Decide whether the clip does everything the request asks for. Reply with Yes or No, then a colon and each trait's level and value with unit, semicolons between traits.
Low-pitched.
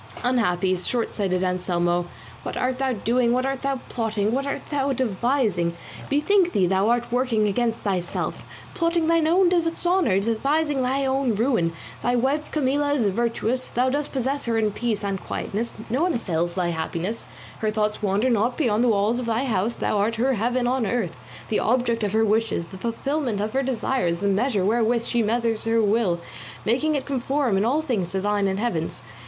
No: high, 235 Hz